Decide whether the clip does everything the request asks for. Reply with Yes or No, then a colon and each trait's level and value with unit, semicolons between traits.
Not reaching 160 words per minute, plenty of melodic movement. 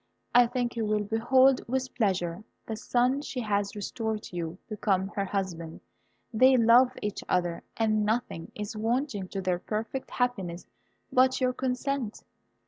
No: average, 150 wpm; average, 4.1 semitones